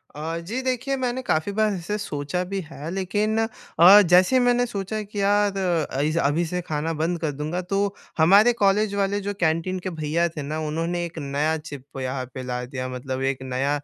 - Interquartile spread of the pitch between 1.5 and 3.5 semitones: No, average, 5.2 semitones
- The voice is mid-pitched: Yes, medium, 175 Hz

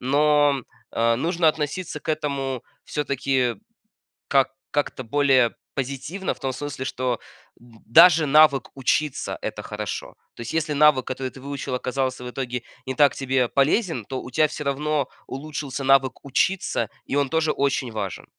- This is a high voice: No, low, 135 Hz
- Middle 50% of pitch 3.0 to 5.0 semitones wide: No, narrow, 2.6 semitones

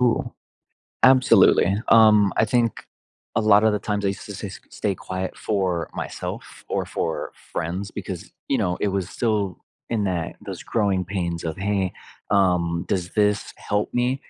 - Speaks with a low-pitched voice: Yes, low, 100 Hz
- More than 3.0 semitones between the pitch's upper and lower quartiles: No, average, 2.7 semitones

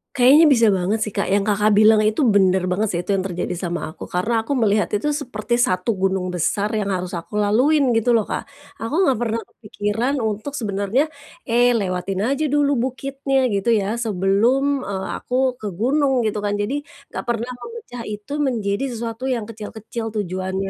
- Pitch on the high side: Yes, high, 215 Hz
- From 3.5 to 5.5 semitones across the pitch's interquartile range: Yes, average, 3.8 semitones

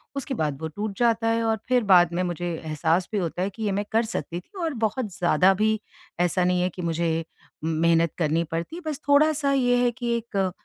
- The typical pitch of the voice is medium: No, high, 195 Hz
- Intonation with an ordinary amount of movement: No, wide, 5.7 semitones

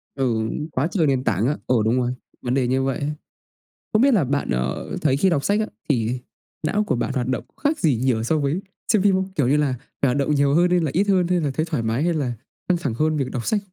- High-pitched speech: No, medium, 140 Hz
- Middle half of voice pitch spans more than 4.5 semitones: Yes, wide, 5.4 semitones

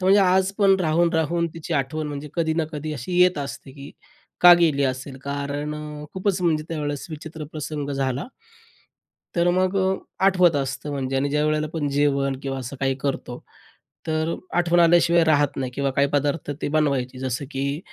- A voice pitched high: No, medium, 150 Hz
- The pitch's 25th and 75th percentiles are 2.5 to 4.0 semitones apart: Yes, average, 3.3 semitones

